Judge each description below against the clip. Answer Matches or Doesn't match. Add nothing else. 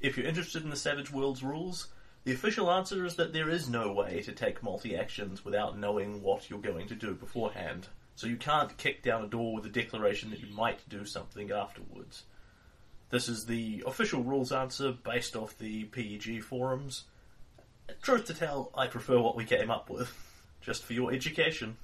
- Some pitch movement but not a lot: Matches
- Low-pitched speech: Matches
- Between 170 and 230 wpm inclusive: Matches